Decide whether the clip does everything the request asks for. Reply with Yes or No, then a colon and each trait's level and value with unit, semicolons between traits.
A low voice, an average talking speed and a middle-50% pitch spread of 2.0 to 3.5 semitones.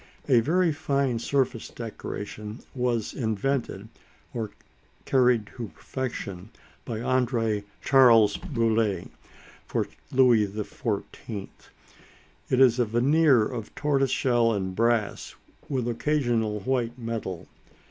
No: low, 120 Hz; slow, 105 wpm; average, 3.2 semitones